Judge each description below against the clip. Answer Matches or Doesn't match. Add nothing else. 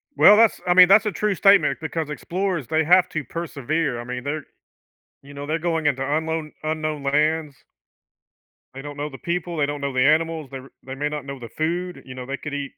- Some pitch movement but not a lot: Matches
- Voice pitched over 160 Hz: Doesn't match